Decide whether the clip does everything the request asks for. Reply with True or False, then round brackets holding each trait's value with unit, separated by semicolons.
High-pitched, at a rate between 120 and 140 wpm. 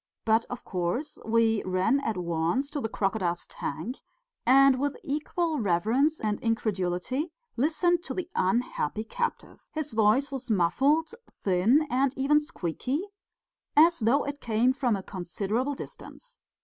True (245 Hz; 135 wpm)